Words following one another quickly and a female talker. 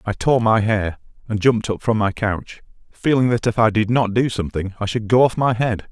No: fast, 245 wpm; male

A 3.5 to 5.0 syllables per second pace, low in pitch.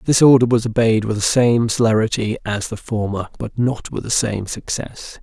Yes: 4.9 syllables/s; low, 115 Hz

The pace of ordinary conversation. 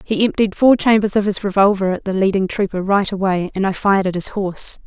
No: fast, 235 wpm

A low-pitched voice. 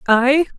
No: very high, 270 Hz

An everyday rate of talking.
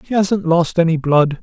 No: fast, 210 wpm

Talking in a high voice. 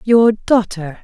Yes: high, 210 Hz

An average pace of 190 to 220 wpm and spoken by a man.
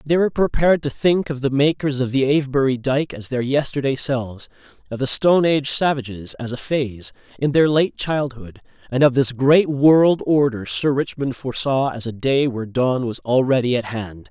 Yes: average, 195 wpm; male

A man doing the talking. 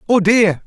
Yes: male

